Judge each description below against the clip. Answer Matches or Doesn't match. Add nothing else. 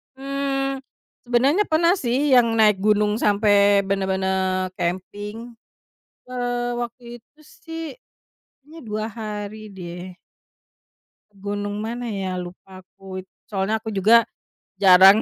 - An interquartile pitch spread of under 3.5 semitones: Doesn't match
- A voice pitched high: Matches